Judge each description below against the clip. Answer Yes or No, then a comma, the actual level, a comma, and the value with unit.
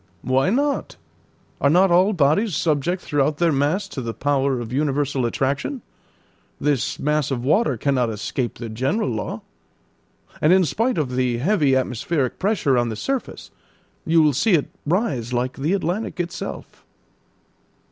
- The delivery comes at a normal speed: Yes, average, 150 wpm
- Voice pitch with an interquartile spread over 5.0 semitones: Yes, wide, 5.4 semitones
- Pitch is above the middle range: No, medium, 145 Hz